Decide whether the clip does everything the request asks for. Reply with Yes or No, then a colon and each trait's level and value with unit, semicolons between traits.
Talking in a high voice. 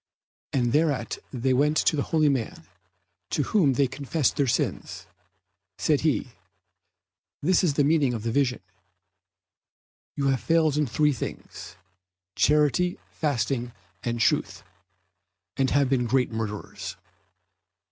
No: medium, 140 Hz